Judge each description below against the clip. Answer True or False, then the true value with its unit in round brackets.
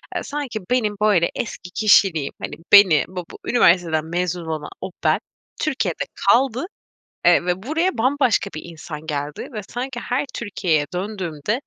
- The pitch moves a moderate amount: False (6.5 semitones)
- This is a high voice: True (195 Hz)